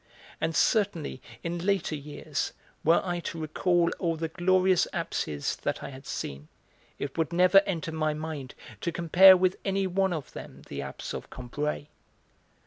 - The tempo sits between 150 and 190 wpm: Yes, average, 160 wpm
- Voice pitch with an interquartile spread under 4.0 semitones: Yes, average, 3.5 semitones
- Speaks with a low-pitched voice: No, medium, 165 Hz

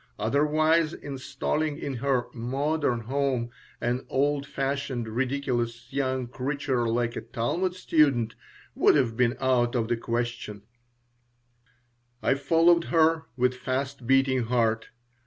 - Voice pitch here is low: Yes, low, 130 Hz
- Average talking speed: No, slow, 120 wpm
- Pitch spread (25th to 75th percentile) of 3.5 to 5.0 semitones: No, average, 3.0 semitones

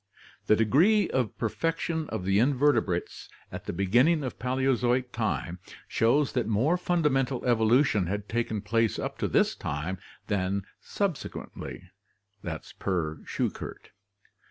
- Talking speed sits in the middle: No, slow, 115 wpm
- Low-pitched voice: Yes, low, 120 Hz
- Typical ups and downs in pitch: No, wide, 5.9 semitones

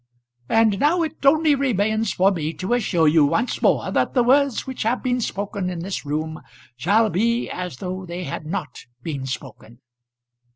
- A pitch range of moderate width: No, wide, 6.9 semitones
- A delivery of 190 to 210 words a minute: No, average, 175 wpm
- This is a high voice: Yes, high, 195 Hz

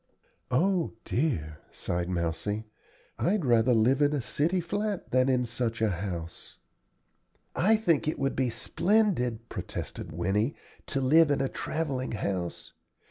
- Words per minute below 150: Yes, slow, 135 wpm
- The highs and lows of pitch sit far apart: Yes, wide, 7.1 semitones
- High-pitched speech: No, low, 125 Hz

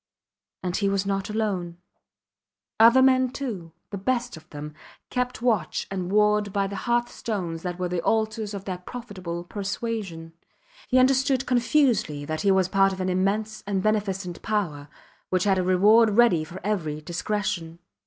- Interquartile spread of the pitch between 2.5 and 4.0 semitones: Yes, average, 3.6 semitones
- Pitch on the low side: No, high, 200 Hz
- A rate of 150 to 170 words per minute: Yes, average, 160 wpm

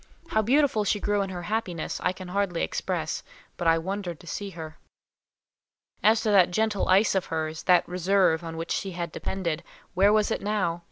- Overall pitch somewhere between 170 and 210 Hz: Yes, medium, 185 Hz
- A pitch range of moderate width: Yes, average, 3.3 semitones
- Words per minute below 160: No, average, 185 wpm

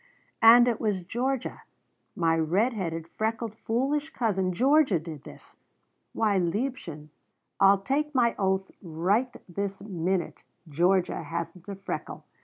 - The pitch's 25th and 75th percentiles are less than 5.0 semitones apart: No, wide, 5.4 semitones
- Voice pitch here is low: No, high, 195 Hz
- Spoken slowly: Yes, slow, 125 wpm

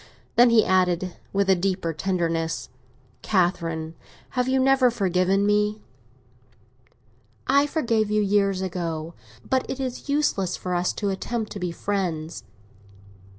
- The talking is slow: Yes, slow, 130 wpm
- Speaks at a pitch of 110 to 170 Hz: No, high, 195 Hz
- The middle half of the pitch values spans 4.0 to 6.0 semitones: Yes, average, 4.4 semitones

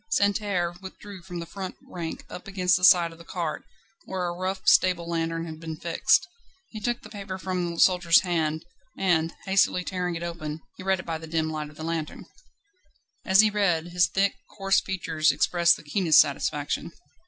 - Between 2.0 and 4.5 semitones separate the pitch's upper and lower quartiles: Yes, narrow, 2.5 semitones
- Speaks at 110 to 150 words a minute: No, average, 190 wpm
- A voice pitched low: No, medium, 175 Hz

